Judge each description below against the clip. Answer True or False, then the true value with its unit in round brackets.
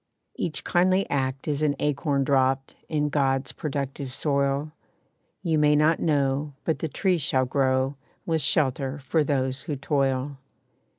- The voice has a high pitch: False (140 Hz)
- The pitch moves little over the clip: True (2.2 semitones)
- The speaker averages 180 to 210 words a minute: False (140 wpm)